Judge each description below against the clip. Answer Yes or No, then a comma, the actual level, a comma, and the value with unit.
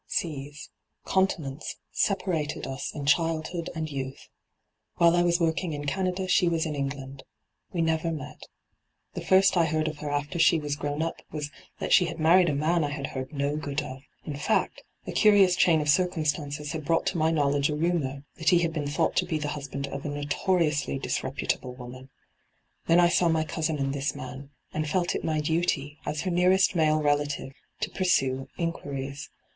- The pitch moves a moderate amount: Yes, average, 3.0 semitones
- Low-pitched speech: No, medium, 155 Hz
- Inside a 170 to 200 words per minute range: Yes, average, 195 wpm